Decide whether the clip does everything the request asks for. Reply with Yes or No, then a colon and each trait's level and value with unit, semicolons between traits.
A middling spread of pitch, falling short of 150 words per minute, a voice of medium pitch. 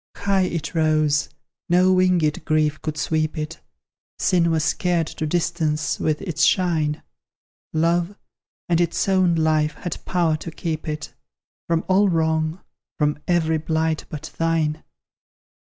No: narrow, 2.0 semitones; slow, 135 wpm; medium, 160 Hz